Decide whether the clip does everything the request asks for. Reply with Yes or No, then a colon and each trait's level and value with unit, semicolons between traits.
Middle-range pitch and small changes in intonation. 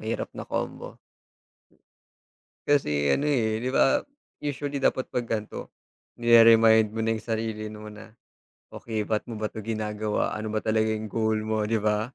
No: low, 110 Hz; narrow, 1.1 semitones